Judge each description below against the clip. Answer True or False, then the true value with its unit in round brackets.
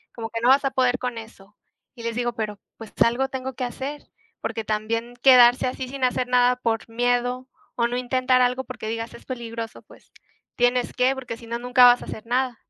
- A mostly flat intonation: True (1.7 semitones)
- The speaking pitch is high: True (245 Hz)